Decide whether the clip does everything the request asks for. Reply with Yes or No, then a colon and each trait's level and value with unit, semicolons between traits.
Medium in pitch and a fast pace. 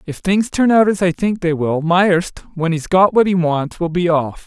Yes: medium, 175 Hz; fast, 255 wpm